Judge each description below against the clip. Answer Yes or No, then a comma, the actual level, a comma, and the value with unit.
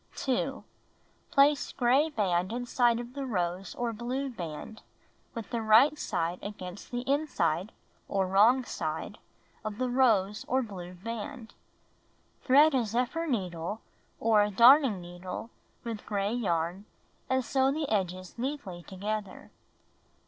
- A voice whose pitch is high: Yes, high, 225 Hz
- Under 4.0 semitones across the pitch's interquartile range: No, average, 5.3 semitones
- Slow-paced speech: Yes, slow, 130 wpm